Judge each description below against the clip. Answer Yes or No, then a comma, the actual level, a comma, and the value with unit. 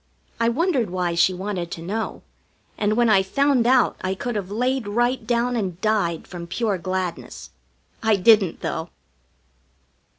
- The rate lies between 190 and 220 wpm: No, average, 155 wpm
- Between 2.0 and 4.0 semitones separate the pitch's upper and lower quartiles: No, average, 4.5 semitones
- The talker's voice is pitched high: Yes, high, 210 Hz